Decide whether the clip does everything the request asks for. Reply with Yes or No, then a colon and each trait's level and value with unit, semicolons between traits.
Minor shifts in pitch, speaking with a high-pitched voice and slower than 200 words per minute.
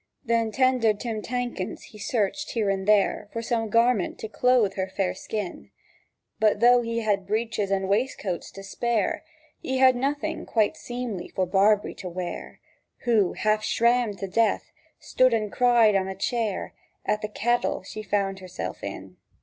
No: average, 3.3 semitones; high, 215 Hz; average, 165 wpm